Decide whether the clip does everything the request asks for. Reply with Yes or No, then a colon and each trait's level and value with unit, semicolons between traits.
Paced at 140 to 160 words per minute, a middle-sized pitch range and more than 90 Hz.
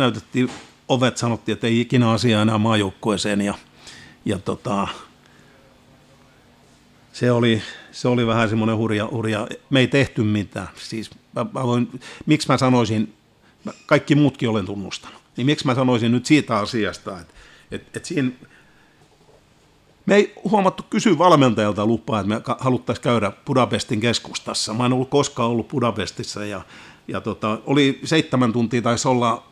Yes: average, 150 wpm; average, 3.0 semitones; low, 120 Hz